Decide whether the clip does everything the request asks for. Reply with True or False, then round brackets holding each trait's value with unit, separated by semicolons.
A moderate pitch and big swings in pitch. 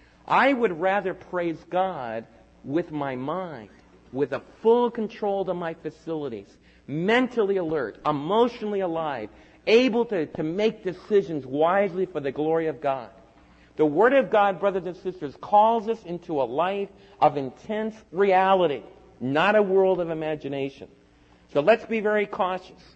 True (175 Hz; 6.0 semitones)